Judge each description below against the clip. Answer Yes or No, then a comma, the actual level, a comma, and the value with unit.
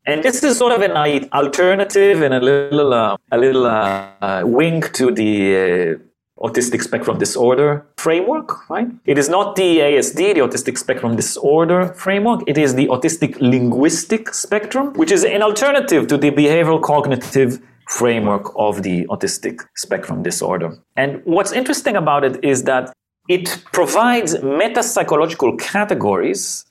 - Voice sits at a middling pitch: Yes, medium, 155 Hz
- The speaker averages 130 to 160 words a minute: Yes, average, 145 wpm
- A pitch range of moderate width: No, wide, 8.4 semitones